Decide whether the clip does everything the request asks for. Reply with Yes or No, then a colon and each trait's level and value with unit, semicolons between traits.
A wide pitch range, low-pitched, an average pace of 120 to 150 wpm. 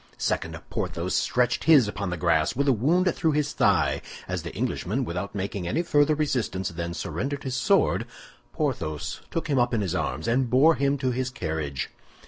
No: wide, 7.9 semitones; low, 125 Hz; average, 185 wpm